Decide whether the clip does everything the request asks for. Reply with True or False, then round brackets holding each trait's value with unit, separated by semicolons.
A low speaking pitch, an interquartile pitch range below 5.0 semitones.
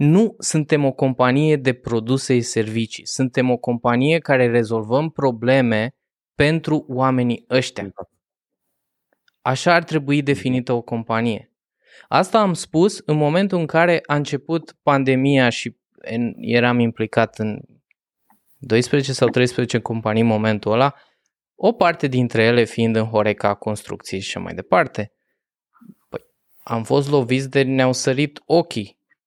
True (130 Hz; 4.1 semitones)